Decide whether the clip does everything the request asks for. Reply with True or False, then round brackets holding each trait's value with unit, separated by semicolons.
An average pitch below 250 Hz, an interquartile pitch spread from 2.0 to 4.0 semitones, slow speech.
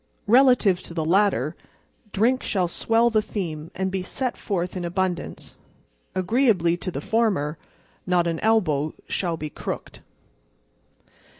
False (185 Hz; 4.5 semitones; 130 wpm)